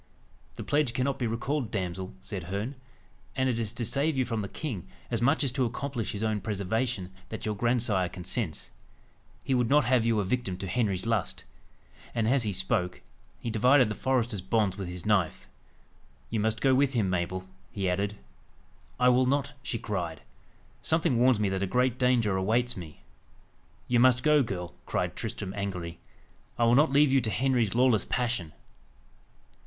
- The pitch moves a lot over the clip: No, average, 4.8 semitones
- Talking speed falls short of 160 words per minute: No, average, 180 wpm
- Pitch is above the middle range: No, low, 115 Hz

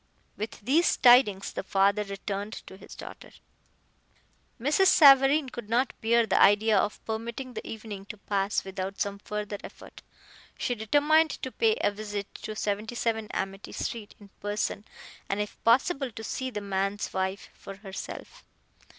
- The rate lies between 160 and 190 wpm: No, average, 150 wpm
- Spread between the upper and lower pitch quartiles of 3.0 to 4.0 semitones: Yes, average, 3.4 semitones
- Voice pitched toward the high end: Yes, high, 215 Hz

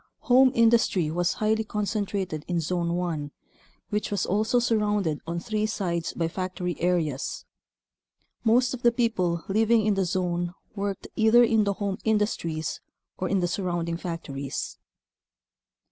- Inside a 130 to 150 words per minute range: Yes, average, 140 wpm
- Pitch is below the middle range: No, high, 190 Hz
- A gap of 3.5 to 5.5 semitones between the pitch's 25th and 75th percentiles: Yes, average, 4.1 semitones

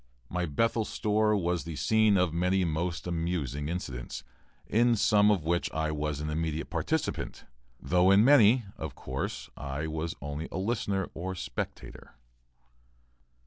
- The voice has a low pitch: Yes, very low, 85 Hz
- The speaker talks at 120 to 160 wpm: Yes, average, 145 wpm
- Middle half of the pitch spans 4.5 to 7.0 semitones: Yes, average, 4.9 semitones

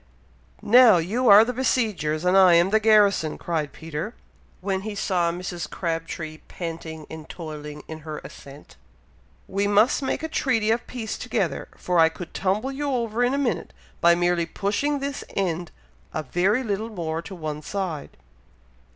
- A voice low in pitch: No, medium, 185 Hz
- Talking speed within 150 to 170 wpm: Yes, average, 165 wpm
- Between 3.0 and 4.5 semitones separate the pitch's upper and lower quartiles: No, average, 5.2 semitones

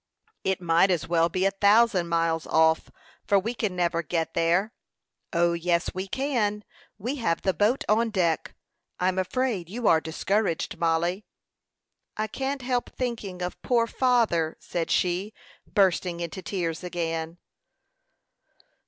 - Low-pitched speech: No, medium, 185 Hz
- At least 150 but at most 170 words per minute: No, average, 140 wpm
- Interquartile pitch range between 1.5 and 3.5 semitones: No, average, 4.3 semitones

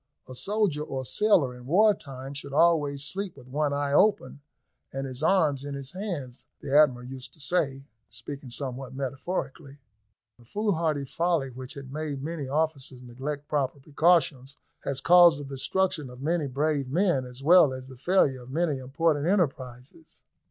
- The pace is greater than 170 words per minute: No, average, 165 wpm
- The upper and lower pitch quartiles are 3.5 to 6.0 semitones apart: Yes, average, 3.8 semitones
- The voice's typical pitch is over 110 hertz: Yes, medium, 140 Hz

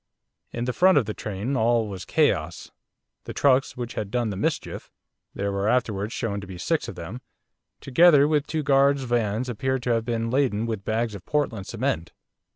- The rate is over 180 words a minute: Yes, average, 190 wpm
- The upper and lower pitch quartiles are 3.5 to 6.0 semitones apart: Yes, average, 4.2 semitones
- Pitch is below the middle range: Yes, low, 120 Hz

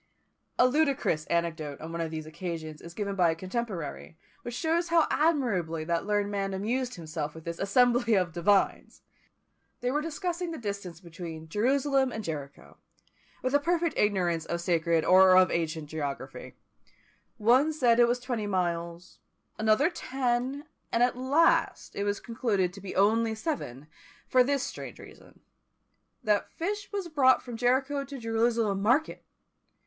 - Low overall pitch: No, high, 210 Hz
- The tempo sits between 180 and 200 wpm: No, average, 155 wpm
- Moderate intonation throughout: No, wide, 7.2 semitones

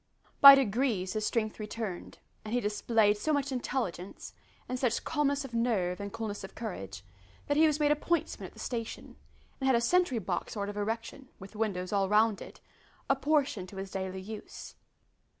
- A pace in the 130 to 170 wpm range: No, average, 185 wpm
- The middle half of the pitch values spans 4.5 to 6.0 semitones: Yes, average, 4.9 semitones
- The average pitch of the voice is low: No, high, 225 Hz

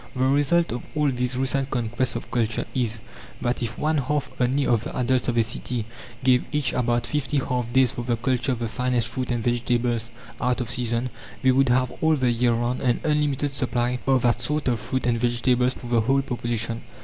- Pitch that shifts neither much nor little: No, narrow, 1.8 semitones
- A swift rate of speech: Yes, fast, 210 wpm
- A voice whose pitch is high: No, low, 125 Hz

